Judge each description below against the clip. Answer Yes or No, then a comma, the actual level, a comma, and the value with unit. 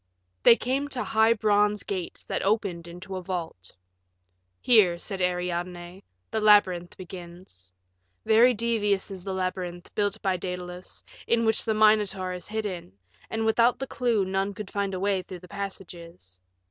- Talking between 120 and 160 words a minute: Yes, average, 155 wpm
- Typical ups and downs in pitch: Yes, average, 3.2 semitones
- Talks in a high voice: Yes, high, 195 Hz